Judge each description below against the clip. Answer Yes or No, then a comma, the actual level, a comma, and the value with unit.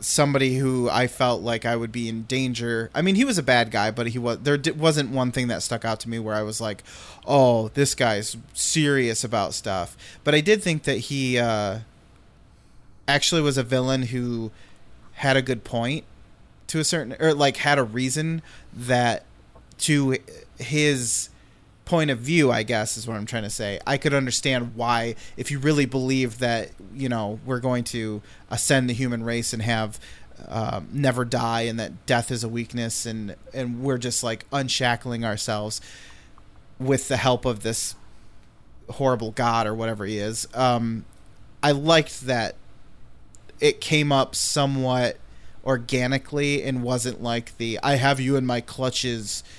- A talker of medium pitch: No, low, 125 Hz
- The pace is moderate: Yes, average, 175 wpm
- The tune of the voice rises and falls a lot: No, average, 3.0 semitones